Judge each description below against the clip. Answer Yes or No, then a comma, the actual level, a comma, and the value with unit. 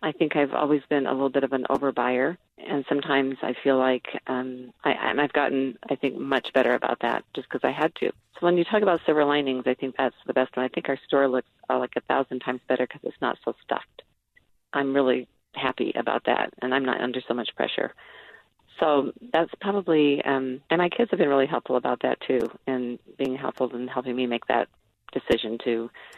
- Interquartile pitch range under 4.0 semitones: Yes, narrow, 2.4 semitones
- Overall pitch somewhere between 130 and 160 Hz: Yes, low, 135 Hz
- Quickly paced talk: Yes, fast, 225 wpm